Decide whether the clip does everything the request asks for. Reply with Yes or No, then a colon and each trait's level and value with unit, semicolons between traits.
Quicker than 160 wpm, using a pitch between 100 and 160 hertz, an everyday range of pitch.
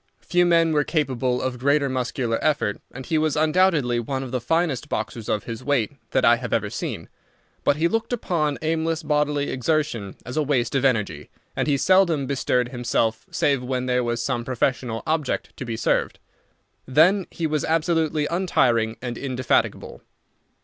Yes: average, 170 wpm; medium, 140 Hz; average, 4.3 semitones